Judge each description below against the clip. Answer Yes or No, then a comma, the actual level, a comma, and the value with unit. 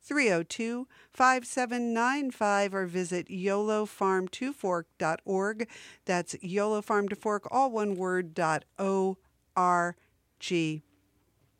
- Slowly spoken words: Yes, slow, 105 wpm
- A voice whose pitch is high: Yes, high, 195 Hz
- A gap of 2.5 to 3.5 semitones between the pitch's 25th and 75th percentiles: No, average, 3.9 semitones